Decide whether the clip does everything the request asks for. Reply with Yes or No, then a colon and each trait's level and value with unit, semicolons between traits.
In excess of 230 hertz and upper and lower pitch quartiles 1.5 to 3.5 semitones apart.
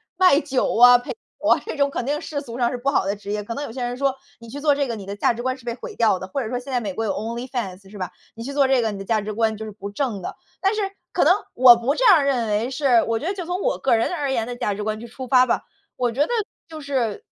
No: high, 245 Hz; average, 4.0 semitones